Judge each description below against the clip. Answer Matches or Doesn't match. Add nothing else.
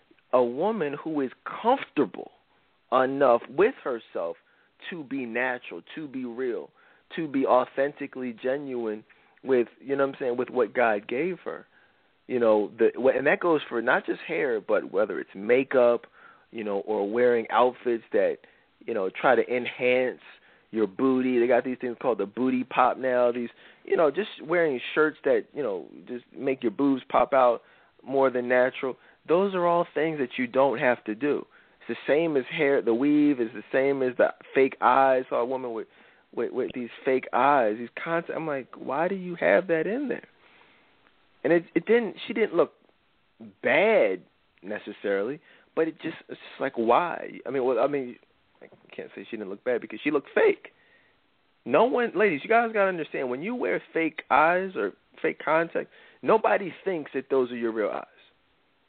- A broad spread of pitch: Matches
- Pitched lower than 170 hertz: Matches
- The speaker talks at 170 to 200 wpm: Matches